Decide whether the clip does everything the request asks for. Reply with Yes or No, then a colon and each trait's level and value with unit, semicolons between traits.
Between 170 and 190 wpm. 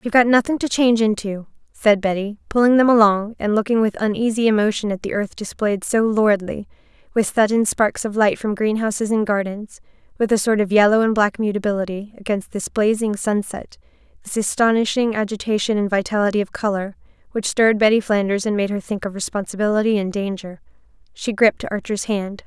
Yes: average, 175 wpm